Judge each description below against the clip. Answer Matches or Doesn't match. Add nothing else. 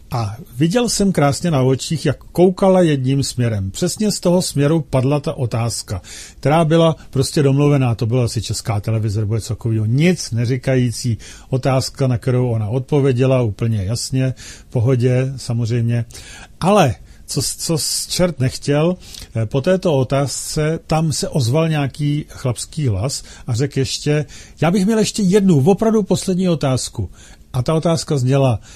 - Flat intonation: Doesn't match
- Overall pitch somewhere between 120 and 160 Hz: Matches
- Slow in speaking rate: Doesn't match